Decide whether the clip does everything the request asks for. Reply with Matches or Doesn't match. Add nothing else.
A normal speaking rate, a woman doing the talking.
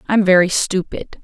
Matches